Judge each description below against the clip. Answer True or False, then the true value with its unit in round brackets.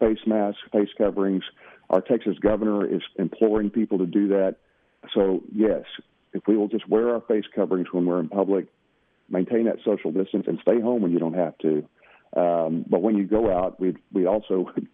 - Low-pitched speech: True (100 Hz)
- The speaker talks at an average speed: True (195 wpm)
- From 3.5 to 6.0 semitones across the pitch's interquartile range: False (2.9 semitones)